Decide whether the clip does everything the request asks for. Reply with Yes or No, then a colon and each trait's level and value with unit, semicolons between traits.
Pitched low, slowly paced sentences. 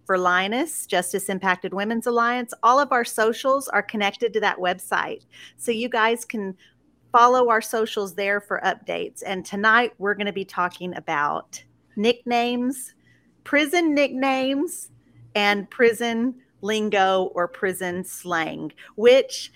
No: high, 215 Hz; slow, 130 wpm